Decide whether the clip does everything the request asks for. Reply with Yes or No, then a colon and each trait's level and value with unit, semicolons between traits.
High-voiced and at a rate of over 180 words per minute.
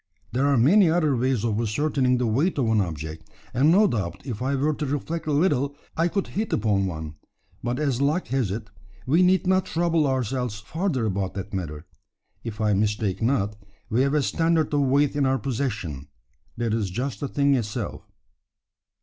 No: low, 130 Hz; average, 190 wpm